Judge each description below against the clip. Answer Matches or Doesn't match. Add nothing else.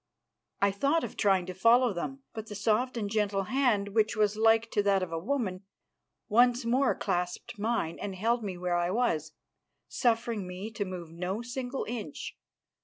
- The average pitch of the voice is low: Doesn't match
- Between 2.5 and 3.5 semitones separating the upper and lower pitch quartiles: Doesn't match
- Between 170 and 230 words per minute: Matches